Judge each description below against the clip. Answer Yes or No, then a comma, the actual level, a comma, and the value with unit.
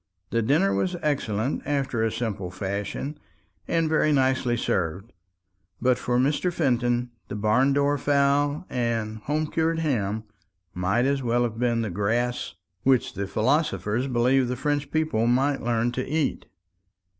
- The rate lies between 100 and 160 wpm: Yes, average, 145 wpm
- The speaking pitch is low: Yes, low, 125 Hz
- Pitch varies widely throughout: No, average, 4.3 semitones